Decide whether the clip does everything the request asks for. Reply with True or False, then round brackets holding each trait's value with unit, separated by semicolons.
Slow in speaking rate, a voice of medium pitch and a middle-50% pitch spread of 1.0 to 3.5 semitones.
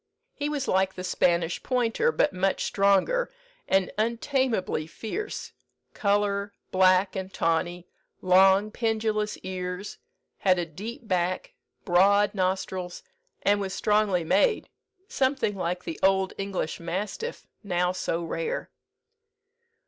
False (115 wpm; 195 Hz; 2.8 semitones)